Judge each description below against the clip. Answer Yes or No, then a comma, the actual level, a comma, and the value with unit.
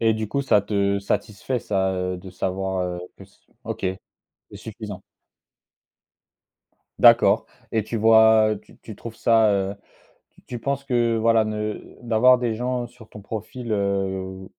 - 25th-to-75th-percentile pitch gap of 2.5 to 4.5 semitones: Yes, average, 2.9 semitones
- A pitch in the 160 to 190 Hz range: No, low, 110 Hz